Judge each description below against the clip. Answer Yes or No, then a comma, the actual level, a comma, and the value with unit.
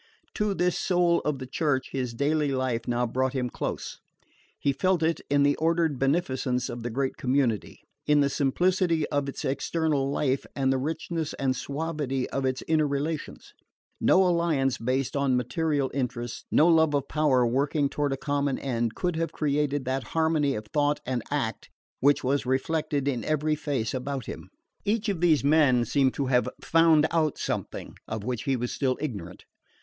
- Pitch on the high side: No, medium, 140 Hz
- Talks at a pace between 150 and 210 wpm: Yes, average, 175 wpm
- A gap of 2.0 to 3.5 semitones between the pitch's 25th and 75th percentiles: Yes, average, 3.2 semitones